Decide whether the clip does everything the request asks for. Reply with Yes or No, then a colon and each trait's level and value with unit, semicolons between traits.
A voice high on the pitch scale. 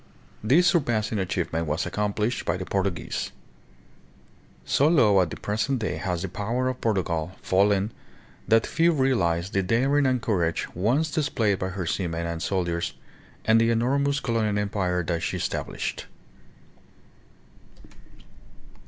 No: low, 105 Hz